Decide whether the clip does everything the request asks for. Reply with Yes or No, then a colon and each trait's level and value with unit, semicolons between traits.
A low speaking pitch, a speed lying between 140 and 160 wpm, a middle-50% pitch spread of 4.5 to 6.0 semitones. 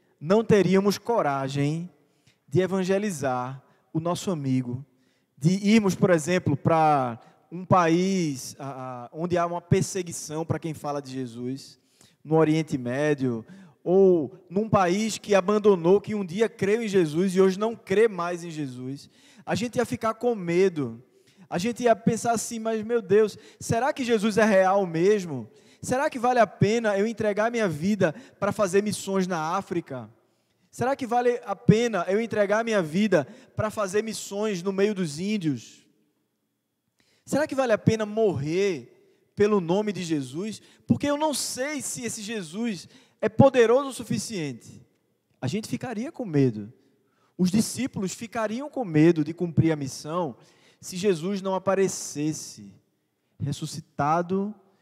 No: high, 190 Hz; average, 150 wpm; wide, 5.5 semitones